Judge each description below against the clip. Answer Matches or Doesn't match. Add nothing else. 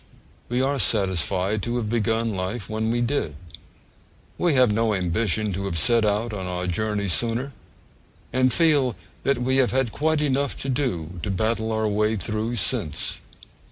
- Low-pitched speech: Matches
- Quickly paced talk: Doesn't match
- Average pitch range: Matches